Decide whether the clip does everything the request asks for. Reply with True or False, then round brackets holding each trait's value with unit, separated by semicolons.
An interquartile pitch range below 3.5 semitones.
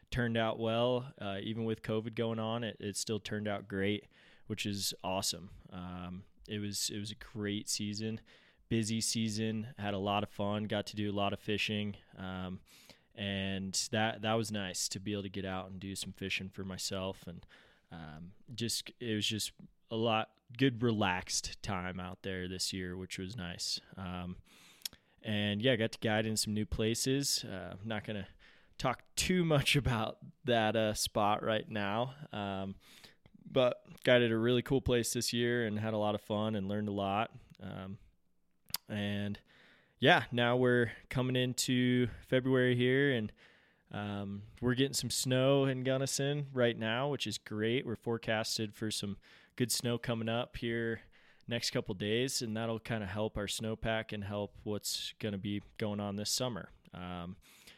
True (3.1 semitones)